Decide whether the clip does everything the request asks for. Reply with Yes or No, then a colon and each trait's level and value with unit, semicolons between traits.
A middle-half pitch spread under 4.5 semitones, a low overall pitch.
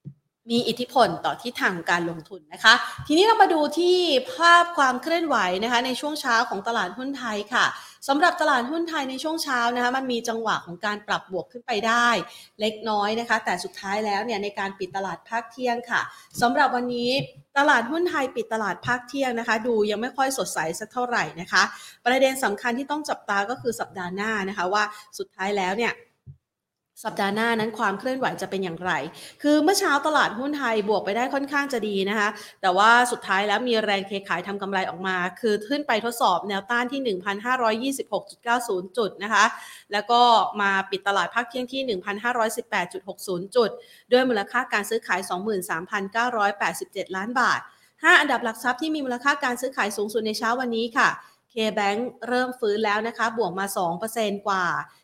No: average, 4.1 semitones; high, 230 Hz